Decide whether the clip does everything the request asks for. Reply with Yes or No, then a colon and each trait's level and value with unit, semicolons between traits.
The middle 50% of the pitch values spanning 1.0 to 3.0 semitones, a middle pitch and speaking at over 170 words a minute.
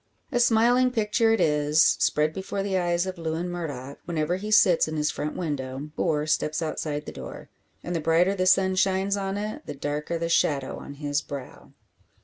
No: average, 4.3 semitones; medium, 170 Hz; average, 190 wpm